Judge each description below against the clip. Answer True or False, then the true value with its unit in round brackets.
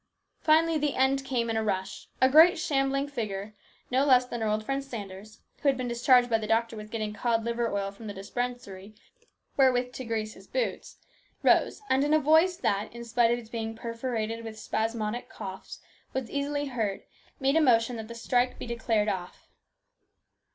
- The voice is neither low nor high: False (235 Hz)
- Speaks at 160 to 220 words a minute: True (190 wpm)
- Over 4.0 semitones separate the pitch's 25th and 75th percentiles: False (3.7 semitones)